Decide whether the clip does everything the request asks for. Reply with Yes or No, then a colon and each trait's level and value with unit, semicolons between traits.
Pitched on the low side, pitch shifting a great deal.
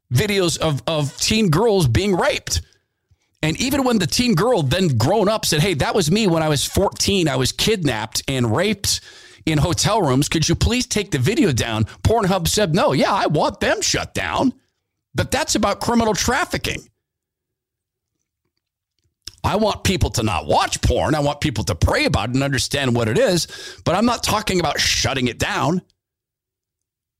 No: medium, 145 Hz; wide, 8.2 semitones